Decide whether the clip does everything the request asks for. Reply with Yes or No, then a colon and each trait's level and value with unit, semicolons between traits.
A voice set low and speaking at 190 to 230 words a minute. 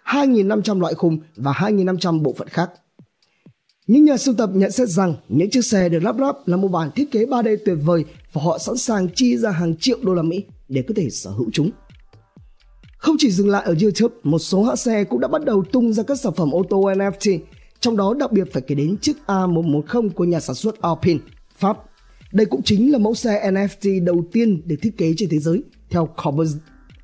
No: high, 195 Hz; average, 220 wpm